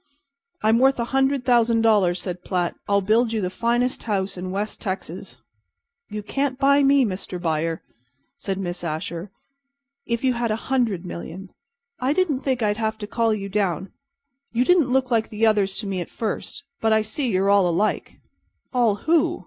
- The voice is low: No, high, 215 Hz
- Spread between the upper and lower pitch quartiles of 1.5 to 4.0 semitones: No, average, 4.6 semitones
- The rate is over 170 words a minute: Yes, average, 180 wpm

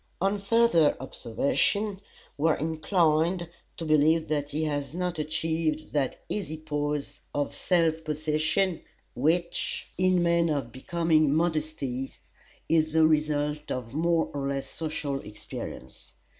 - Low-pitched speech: No, medium, 155 Hz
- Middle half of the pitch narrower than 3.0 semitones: Yes, narrow, 2.4 semitones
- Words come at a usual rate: No, slow, 125 wpm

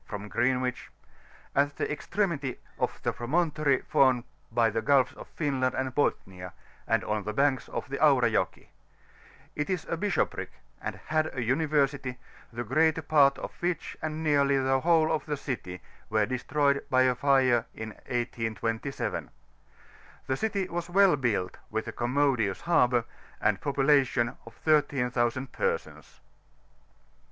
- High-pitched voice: No, low, 135 Hz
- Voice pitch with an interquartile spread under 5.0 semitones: Yes, average, 4.0 semitones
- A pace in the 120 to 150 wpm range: Yes, average, 145 wpm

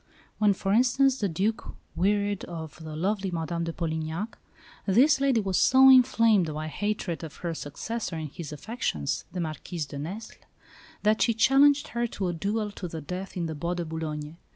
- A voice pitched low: No, medium, 185 Hz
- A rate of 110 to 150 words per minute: No, average, 180 wpm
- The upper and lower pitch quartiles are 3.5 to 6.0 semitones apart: Yes, wide, 5.4 semitones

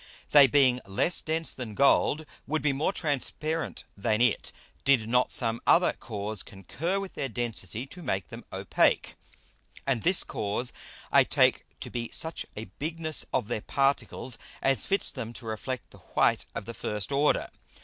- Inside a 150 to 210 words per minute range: Yes, average, 165 wpm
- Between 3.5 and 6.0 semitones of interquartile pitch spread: Yes, wide, 5.4 semitones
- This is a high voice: No, low, 130 Hz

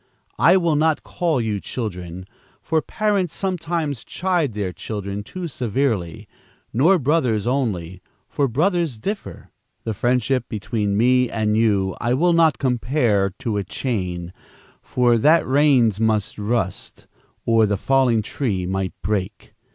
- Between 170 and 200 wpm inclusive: No, slow, 135 wpm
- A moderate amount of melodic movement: No, wide, 6.3 semitones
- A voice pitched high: No, low, 120 Hz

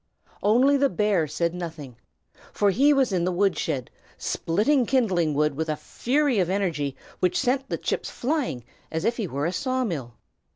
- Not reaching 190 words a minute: Yes, average, 180 wpm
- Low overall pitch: No, high, 190 Hz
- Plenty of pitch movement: Yes, wide, 7.8 semitones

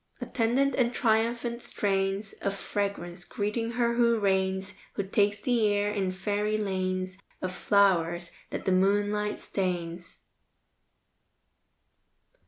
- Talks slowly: Yes, slow, 110 wpm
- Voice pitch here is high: Yes, high, 200 Hz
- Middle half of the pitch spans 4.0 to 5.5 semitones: No, average, 2.7 semitones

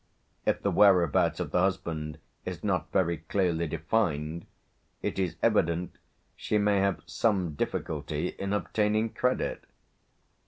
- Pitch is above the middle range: No, very low, 90 Hz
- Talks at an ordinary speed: No, slow, 125 wpm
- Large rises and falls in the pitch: No, average, 3.7 semitones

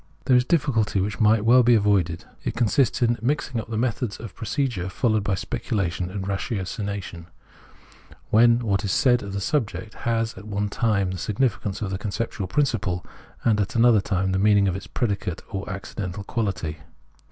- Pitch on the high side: No, low, 105 Hz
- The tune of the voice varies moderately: Yes, average, 3.3 semitones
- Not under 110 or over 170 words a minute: No, average, 180 wpm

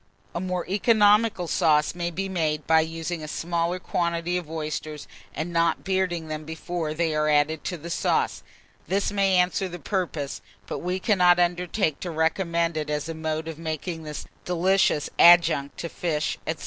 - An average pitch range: No, narrow, 2.3 semitones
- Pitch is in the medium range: Yes, medium, 170 Hz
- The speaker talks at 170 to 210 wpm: Yes, average, 175 wpm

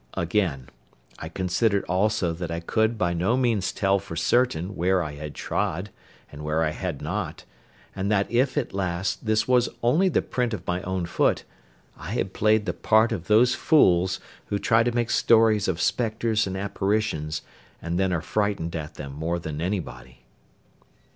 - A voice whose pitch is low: Yes, very low, 95 Hz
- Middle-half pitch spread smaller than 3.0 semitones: No, average, 4.5 semitones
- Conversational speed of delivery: Yes, average, 175 wpm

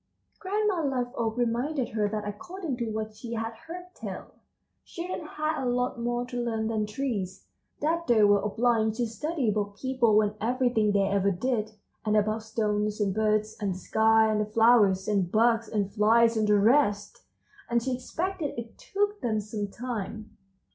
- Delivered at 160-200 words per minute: Yes, average, 175 wpm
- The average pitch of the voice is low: No, high, 225 Hz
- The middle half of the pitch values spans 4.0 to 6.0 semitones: No, average, 2.9 semitones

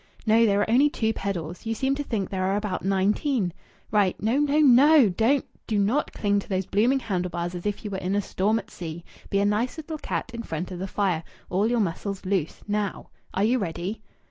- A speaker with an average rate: No, fast, 225 wpm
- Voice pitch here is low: No, high, 205 Hz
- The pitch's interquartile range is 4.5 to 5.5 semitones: No, average, 3.8 semitones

